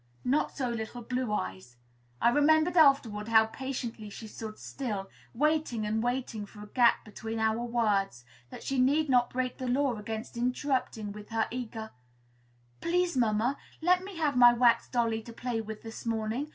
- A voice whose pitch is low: No, high, 235 Hz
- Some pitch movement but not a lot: Yes, average, 3.2 semitones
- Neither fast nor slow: Yes, average, 170 wpm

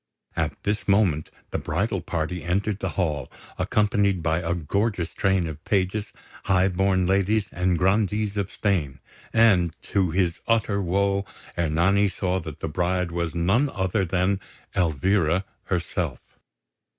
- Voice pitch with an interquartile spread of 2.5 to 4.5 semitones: Yes, average, 2.8 semitones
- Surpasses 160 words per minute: No, average, 140 wpm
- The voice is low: Yes, very low, 95 Hz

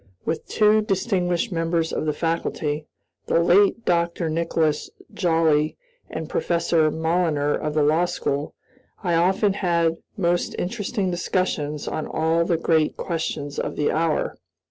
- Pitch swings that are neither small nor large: No, narrow, 2.2 semitones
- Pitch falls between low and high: Yes, medium, 165 Hz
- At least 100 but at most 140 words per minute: Yes, slow, 135 wpm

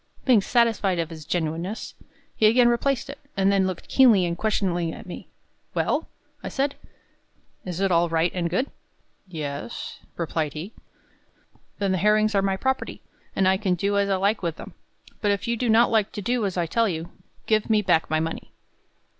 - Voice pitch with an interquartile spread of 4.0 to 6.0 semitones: Yes, average, 4.3 semitones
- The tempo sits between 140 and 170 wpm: No, average, 190 wpm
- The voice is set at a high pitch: Yes, high, 195 Hz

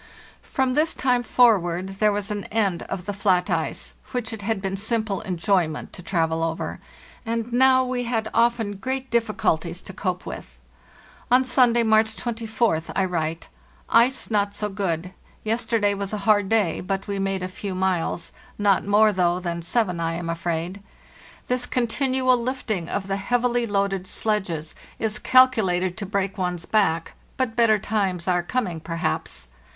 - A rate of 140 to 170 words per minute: Yes, average, 160 wpm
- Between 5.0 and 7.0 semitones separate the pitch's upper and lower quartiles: No, average, 4.2 semitones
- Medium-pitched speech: No, high, 205 Hz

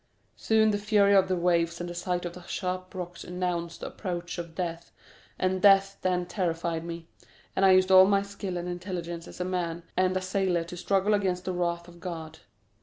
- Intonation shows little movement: Yes, narrow, 1.7 semitones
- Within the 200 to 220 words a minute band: Yes, fast, 205 wpm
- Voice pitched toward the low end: No, medium, 180 Hz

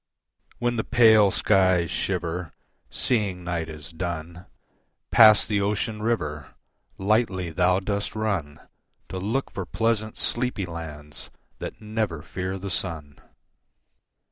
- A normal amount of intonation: Yes, average, 4.3 semitones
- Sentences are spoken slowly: Yes, slow, 115 wpm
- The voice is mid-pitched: No, very low, 95 Hz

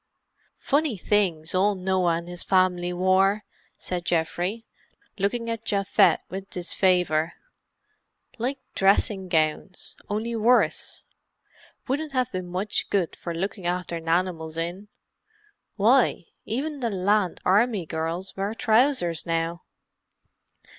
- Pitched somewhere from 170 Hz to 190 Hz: Yes, medium, 185 Hz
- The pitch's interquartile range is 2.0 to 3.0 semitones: No, average, 3.5 semitones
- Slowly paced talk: Yes, slow, 115 wpm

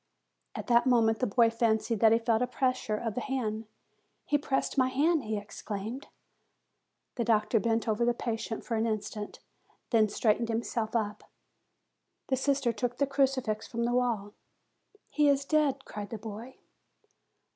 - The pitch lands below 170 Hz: No, high, 230 Hz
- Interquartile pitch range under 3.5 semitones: Yes, average, 2.8 semitones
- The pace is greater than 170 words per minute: No, average, 165 wpm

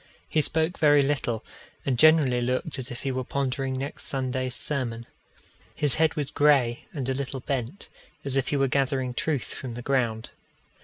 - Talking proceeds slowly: No, average, 175 wpm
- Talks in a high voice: No, low, 135 Hz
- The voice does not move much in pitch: Yes, narrow, 2.3 semitones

